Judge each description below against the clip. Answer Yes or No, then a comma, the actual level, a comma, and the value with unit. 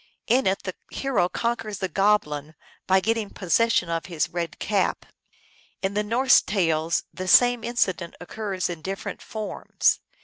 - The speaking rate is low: No, average, 145 wpm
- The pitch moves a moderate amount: Yes, average, 4.3 semitones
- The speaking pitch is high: Yes, high, 195 Hz